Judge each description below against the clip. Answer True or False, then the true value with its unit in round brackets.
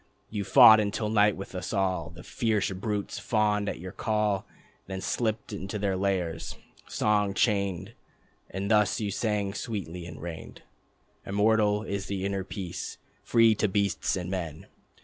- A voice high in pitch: False (100 Hz)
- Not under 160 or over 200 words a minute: False (150 wpm)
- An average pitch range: False (2.0 semitones)